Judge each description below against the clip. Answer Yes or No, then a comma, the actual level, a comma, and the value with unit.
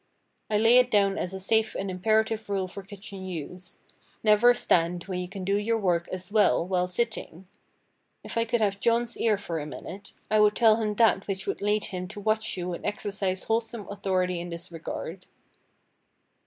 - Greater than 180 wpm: Yes, average, 190 wpm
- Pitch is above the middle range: Yes, high, 200 Hz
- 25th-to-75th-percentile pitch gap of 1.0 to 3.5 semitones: Yes, average, 3.1 semitones